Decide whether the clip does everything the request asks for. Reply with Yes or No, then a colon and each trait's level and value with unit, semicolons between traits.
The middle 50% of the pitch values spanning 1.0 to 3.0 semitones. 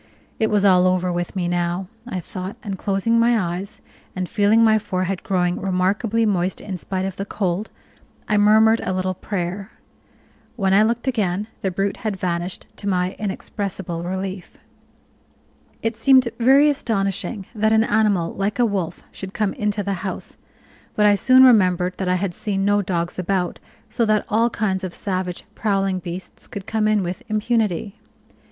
Yes: average, 2.7 semitones